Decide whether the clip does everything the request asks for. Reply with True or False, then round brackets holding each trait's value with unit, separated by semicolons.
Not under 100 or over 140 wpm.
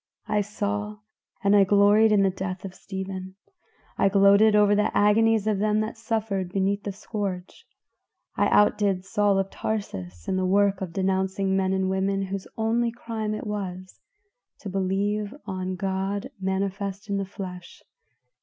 False (155 wpm)